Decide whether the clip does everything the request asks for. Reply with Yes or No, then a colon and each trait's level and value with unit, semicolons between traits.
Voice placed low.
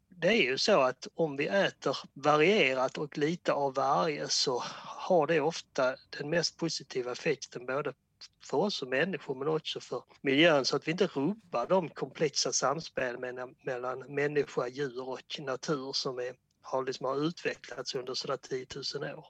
No: medium, 145 Hz